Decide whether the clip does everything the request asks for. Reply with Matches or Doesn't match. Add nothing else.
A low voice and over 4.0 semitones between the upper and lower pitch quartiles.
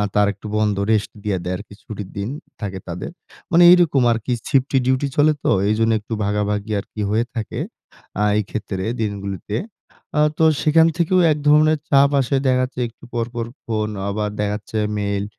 Matches